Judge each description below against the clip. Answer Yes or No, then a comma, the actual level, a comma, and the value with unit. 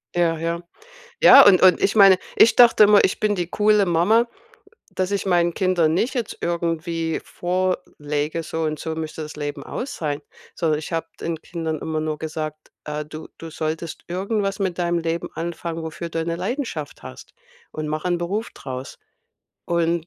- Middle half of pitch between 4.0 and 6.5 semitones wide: No, average, 2.9 semitones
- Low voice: No, medium, 170 Hz